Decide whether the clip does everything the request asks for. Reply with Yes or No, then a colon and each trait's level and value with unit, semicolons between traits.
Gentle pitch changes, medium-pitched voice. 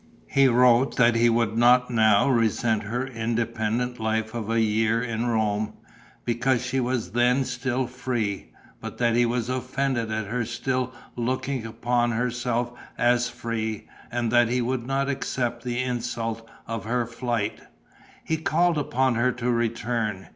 No: narrow, 1.7 semitones; low, 120 Hz